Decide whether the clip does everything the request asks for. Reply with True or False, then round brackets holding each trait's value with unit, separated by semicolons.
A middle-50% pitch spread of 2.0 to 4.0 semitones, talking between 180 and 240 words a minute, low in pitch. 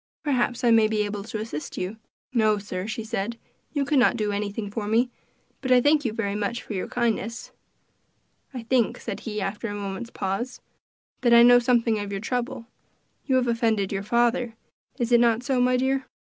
False (2.8 semitones; 200 wpm; 230 Hz)